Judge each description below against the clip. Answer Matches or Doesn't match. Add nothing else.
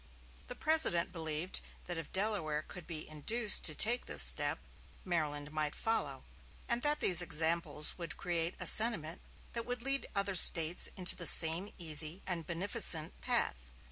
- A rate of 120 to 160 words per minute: Matches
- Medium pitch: Matches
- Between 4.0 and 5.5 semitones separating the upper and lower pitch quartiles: Matches